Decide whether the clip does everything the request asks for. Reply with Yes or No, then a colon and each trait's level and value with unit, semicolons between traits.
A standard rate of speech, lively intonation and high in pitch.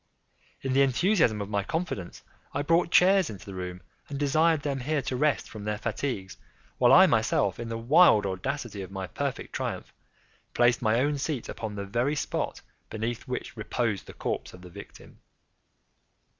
No: average, 175 wpm; wide, 5.9 semitones; low, 120 Hz